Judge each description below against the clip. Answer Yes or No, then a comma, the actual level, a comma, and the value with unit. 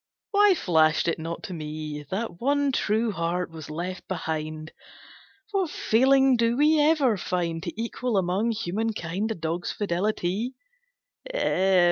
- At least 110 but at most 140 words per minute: Yes, slow, 135 wpm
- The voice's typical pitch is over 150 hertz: Yes, high, 190 Hz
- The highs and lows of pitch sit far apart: Yes, wide, 6.0 semitones